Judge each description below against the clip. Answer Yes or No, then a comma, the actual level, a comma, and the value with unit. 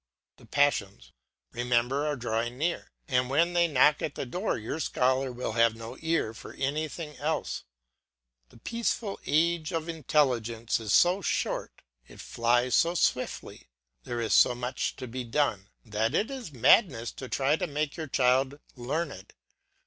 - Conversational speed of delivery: Yes, average, 155 wpm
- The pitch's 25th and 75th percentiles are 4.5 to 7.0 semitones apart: Yes, average, 4.9 semitones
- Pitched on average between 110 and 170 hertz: Yes, low, 135 Hz